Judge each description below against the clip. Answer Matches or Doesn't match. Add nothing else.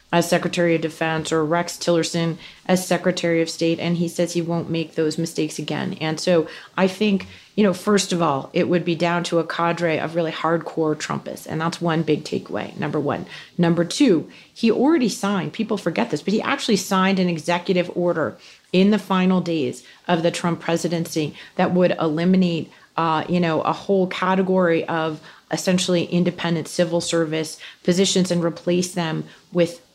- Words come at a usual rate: Matches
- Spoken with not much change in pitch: Matches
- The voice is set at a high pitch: Doesn't match